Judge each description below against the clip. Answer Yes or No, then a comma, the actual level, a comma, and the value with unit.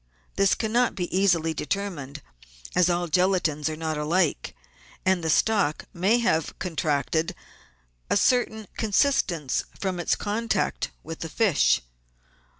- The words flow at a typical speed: No, slow, 125 wpm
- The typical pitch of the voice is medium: Yes, medium, 175 Hz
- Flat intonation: No, average, 4.2 semitones